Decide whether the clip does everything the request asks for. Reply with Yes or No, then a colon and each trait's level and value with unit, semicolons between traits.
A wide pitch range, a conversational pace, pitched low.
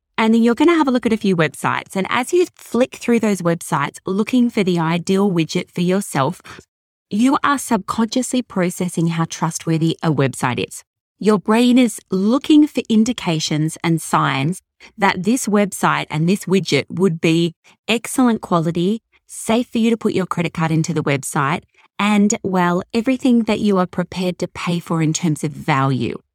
No: wide, 5.7 semitones; average, 180 wpm; medium, 185 Hz